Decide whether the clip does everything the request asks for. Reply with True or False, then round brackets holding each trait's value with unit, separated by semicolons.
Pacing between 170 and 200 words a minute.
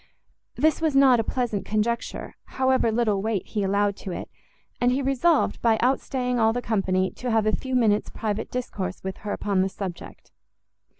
True (180 wpm)